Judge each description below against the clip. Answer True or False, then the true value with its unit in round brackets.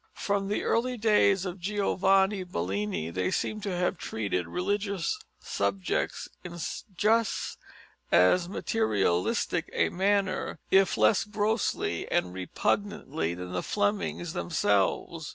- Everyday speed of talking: False (115 wpm)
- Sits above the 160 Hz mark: True (190 Hz)